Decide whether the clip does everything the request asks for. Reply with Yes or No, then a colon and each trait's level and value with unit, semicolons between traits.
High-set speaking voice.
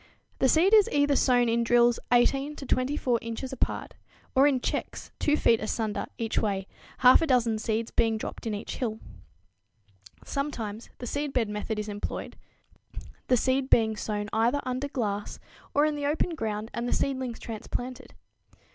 Yes: high, 245 Hz